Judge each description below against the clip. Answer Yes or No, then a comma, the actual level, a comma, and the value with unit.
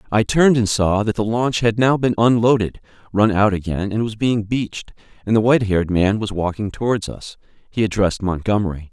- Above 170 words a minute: Yes, average, 200 wpm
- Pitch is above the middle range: No, low, 105 Hz